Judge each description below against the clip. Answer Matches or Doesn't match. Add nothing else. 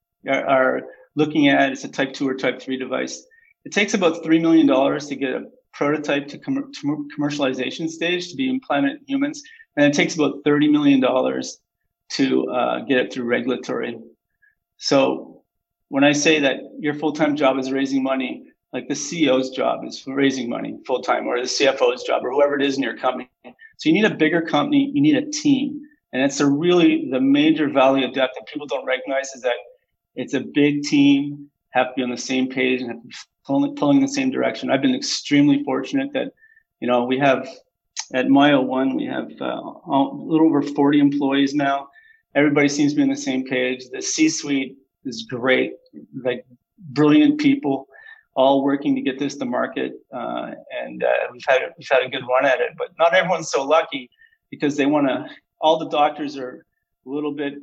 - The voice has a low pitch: Doesn't match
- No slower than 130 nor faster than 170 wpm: Doesn't match